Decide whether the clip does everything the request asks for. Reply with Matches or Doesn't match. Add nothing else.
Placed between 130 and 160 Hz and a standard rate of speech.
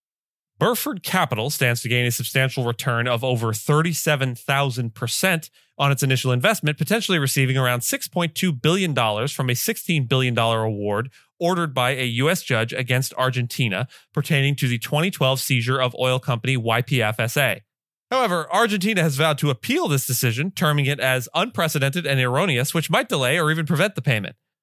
Matches